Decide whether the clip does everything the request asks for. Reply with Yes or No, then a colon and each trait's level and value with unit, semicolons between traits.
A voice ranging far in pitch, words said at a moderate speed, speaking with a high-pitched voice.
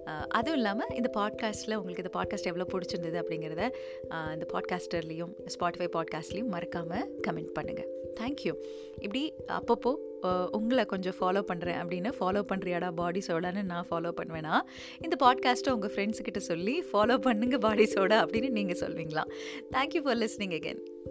No: wide, 6.0 semitones; fast, 135 wpm; high, 195 Hz